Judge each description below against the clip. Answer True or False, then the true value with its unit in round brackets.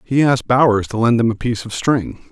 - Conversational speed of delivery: False (260 wpm)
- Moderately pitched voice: False (120 Hz)